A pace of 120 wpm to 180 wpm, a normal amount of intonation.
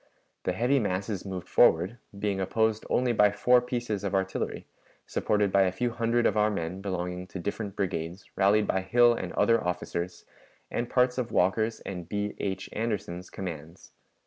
Yes: average, 170 wpm; average, 3.7 semitones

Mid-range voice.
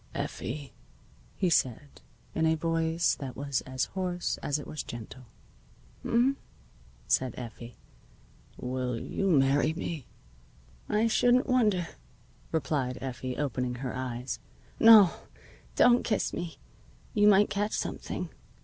Yes: medium, 150 Hz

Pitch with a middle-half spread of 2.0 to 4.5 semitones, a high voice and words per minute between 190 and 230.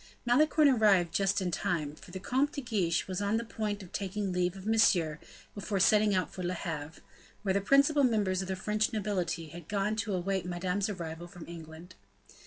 Yes: average, 3.3 semitones; high, 195 Hz; average, 195 wpm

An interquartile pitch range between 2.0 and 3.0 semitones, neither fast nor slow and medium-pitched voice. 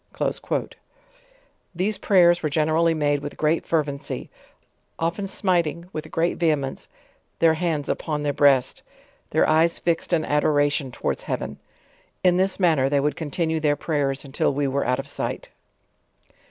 Yes: average, 2.7 semitones; average, 145 wpm; medium, 155 Hz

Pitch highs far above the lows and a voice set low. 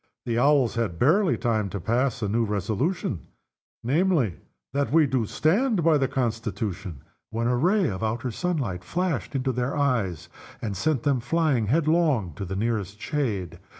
Yes: wide, 6.1 semitones; low, 120 Hz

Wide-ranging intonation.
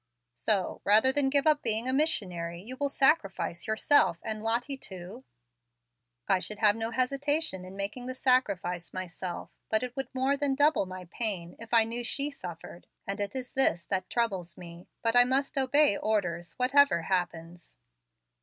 Yes: wide, 6.3 semitones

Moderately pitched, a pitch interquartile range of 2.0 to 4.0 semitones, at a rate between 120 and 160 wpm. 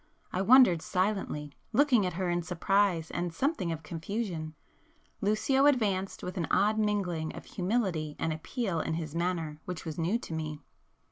No: medium, 180 Hz; average, 4.5 semitones; average, 155 wpm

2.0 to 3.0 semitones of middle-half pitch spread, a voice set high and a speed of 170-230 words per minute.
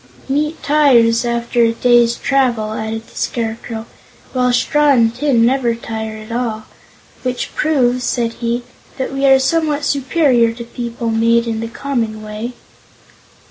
No: narrow, 2.6 semitones; high, 235 Hz; average, 145 wpm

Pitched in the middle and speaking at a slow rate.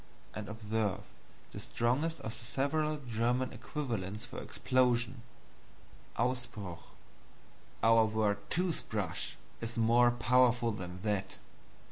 No: low, 115 Hz; slow, 100 wpm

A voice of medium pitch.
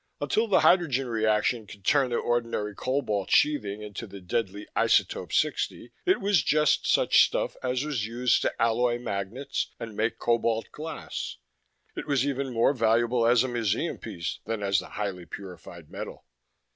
No: low, 115 Hz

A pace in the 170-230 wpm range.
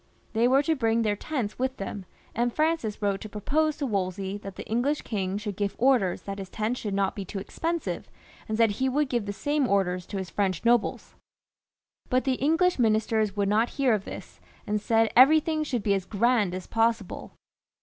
Yes: average, 200 wpm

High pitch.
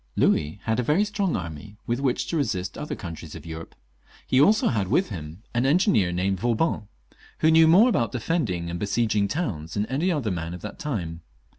No: low, 110 Hz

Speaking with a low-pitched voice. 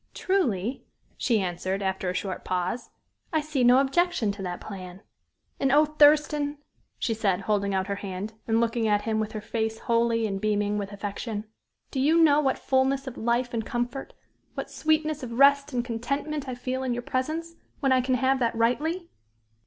No: high, 240 Hz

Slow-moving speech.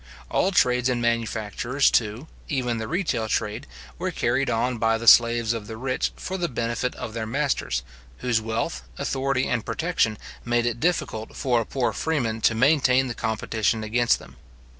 No: average, 170 wpm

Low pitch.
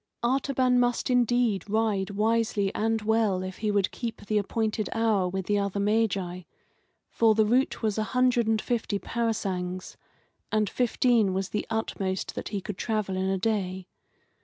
No: high, 215 Hz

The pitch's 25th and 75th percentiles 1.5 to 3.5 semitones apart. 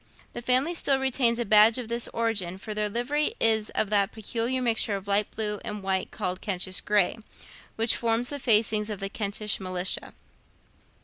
Yes: average, 2.8 semitones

